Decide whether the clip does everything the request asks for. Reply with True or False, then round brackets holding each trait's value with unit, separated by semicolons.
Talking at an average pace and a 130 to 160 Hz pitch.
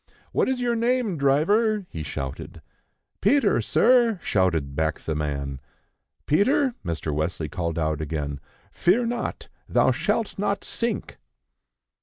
False (125 wpm; 140 Hz)